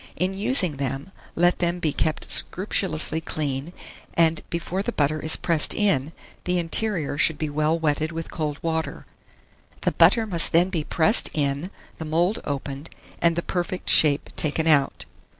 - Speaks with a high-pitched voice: No, medium, 160 Hz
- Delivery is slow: No, average, 160 wpm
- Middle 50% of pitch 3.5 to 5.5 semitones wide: No, average, 2.8 semitones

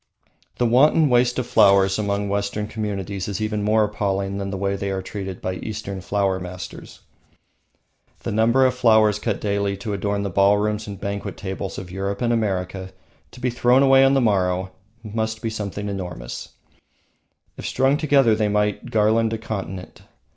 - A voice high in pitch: No, low, 105 Hz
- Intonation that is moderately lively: No, narrow, 2.3 semitones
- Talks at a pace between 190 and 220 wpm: No, average, 170 wpm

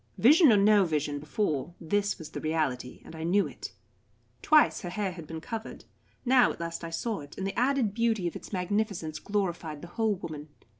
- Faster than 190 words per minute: Yes, average, 200 wpm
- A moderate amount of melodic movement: Yes, average, 4.9 semitones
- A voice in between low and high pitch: Yes, medium, 180 Hz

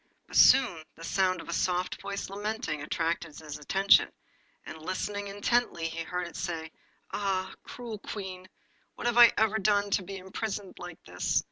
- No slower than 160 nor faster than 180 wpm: Yes, average, 165 wpm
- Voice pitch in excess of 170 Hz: Yes, medium, 185 Hz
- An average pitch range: Yes, average, 3.5 semitones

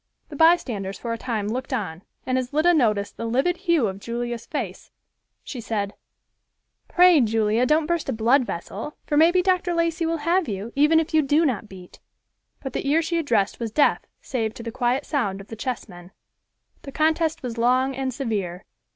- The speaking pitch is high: Yes, very high, 255 Hz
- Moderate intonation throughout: No, wide, 6.1 semitones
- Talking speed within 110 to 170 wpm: No, average, 190 wpm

